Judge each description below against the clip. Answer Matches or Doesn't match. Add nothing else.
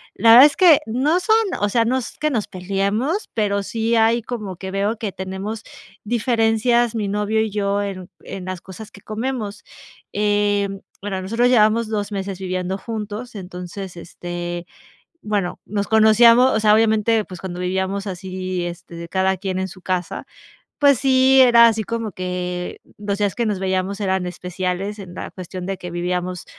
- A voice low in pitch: Doesn't match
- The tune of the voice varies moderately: Matches